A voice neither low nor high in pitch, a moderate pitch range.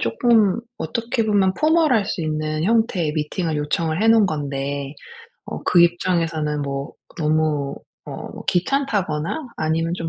No: medium, 165 Hz; wide, 5.8 semitones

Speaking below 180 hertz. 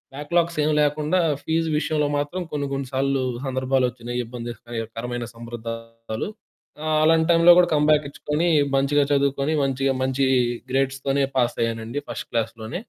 Yes: low, 135 Hz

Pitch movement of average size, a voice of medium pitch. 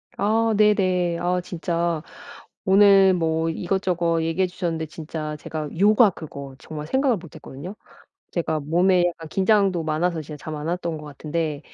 Yes: average, 3.1 semitones; medium, 170 Hz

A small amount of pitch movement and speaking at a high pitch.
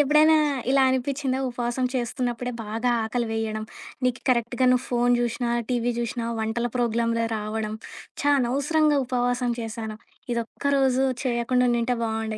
Yes: narrow, 1.9 semitones; high, 240 Hz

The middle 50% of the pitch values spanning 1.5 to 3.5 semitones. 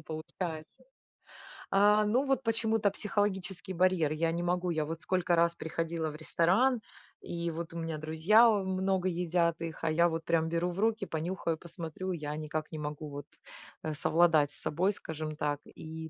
Yes: average, 3.0 semitones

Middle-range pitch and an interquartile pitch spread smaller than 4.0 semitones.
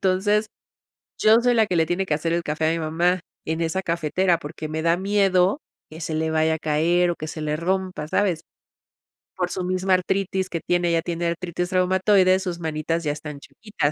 Yes: medium, 175 Hz; average, 2.8 semitones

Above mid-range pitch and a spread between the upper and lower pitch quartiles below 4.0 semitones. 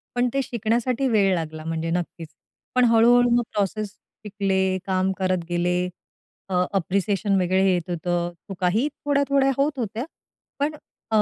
No: high, 195 Hz; average, 5.2 semitones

